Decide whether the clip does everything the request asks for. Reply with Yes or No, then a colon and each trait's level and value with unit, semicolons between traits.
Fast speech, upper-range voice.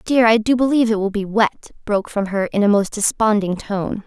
Yes: fast, 235 wpm; high, 210 Hz